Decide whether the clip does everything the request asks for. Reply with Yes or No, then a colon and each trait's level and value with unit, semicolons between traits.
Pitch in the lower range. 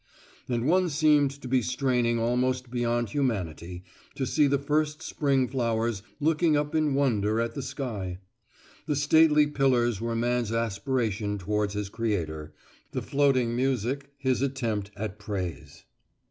Yes: low, 125 Hz